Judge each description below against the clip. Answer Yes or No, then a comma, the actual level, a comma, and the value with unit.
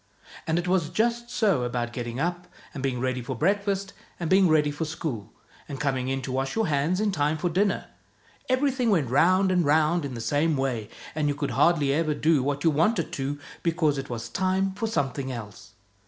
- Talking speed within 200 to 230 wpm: Yes, fast, 205 wpm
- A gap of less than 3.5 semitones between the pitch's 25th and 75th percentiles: No, wide, 5.5 semitones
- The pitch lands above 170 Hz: No, medium, 155 Hz